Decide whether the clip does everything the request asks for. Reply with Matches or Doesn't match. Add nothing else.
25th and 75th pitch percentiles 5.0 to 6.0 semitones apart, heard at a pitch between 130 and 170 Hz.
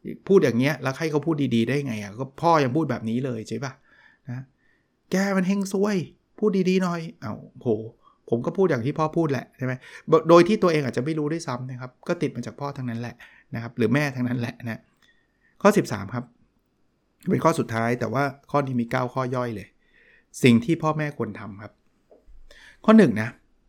Matches